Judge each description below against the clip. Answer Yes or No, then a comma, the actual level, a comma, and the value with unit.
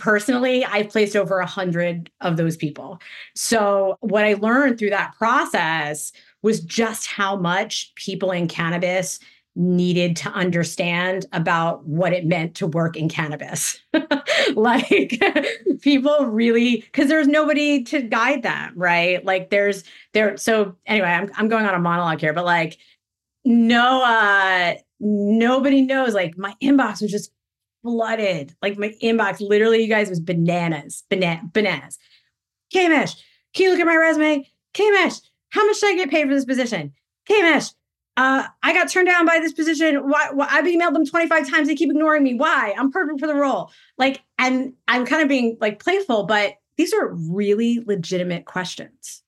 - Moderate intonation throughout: No, wide, 7.5 semitones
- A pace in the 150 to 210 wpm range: Yes, average, 165 wpm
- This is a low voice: No, high, 220 Hz